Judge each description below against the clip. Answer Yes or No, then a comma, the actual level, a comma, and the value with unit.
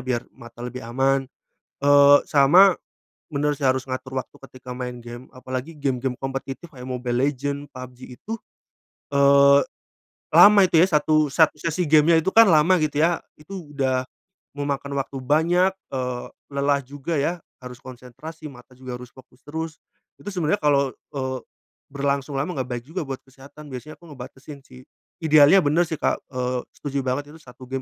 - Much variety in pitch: No, average, 3.0 semitones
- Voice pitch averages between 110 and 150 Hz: Yes, medium, 140 Hz